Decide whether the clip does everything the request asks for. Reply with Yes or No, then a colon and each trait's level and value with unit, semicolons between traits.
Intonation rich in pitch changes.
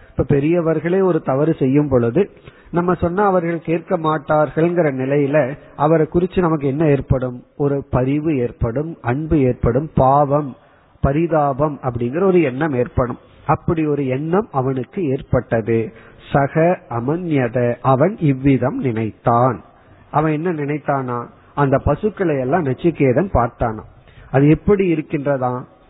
No: average, 4.2 semitones